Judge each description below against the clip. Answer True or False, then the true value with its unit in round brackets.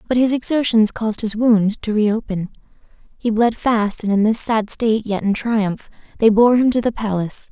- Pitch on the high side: True (220 Hz)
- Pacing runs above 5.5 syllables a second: False (5.1 syllables/s)